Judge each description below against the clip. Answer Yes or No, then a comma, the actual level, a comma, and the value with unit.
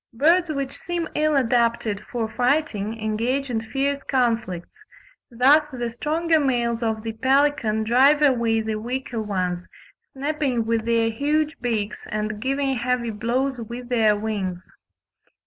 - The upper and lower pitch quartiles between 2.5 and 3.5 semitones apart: No, average, 3.9 semitones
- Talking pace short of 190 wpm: Yes, slow, 135 wpm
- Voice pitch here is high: Yes, high, 240 Hz